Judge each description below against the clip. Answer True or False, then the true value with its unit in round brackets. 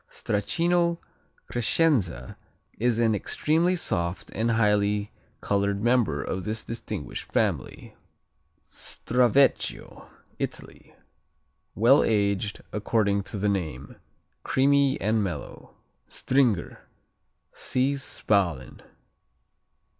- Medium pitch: False (110 Hz)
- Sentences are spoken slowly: True (85 wpm)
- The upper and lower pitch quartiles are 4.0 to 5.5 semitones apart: True (4.6 semitones)